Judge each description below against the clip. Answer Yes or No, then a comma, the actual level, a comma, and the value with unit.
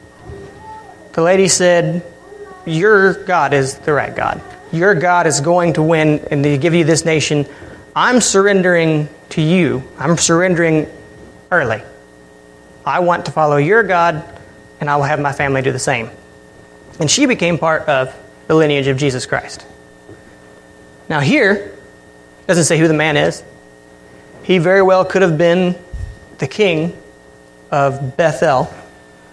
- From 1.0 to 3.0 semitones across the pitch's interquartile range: No, wide, 5.5 semitones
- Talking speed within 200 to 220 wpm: No, average, 145 wpm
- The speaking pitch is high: No, medium, 155 Hz